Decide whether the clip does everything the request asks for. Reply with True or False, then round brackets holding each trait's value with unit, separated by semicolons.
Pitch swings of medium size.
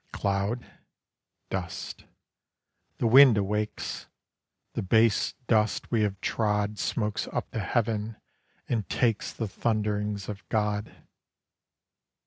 False (1.6 semitones)